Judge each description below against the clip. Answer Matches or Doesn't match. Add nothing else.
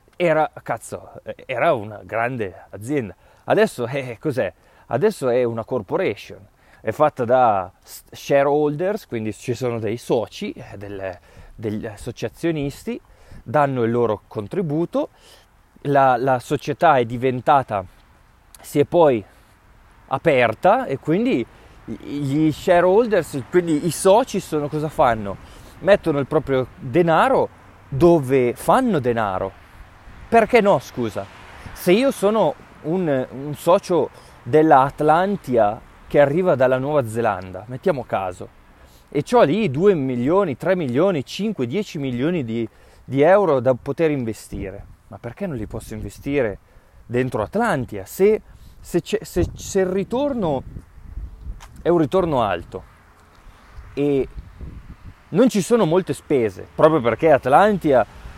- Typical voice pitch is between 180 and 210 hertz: Doesn't match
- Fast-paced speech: Doesn't match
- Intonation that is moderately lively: Doesn't match